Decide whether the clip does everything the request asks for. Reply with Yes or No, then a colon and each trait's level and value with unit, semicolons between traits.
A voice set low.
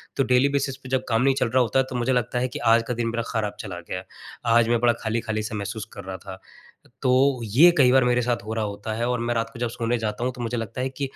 Yes: low, 120 Hz